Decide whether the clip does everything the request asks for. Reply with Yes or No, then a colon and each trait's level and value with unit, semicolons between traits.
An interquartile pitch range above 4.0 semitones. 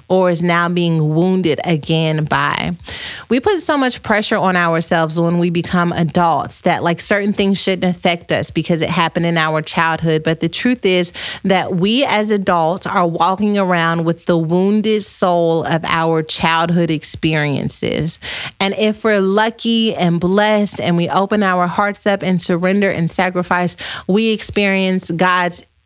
No: average, 3.0 semitones